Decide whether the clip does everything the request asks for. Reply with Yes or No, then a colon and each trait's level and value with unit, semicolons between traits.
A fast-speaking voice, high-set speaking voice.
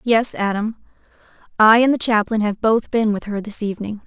No: average, 190 wpm; high, 215 Hz